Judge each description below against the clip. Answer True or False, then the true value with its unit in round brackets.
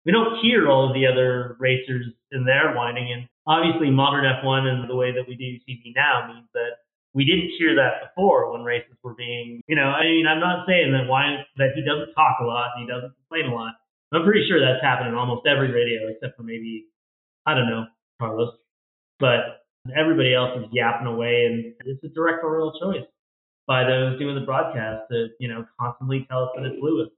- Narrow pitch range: False (3.1 semitones)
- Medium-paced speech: False (215 wpm)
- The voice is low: True (130 Hz)